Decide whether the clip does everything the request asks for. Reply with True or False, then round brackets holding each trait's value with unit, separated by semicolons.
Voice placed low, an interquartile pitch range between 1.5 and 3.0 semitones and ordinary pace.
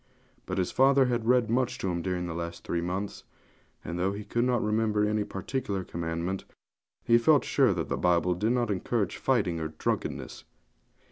False (100 Hz; 5.1 semitones; 185 wpm)